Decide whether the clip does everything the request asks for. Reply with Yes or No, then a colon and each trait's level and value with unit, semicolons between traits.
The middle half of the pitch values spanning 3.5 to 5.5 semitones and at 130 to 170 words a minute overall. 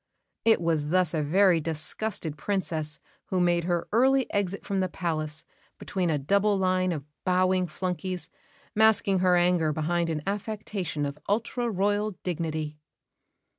Yes: average, 3.9 semitones; average, 140 wpm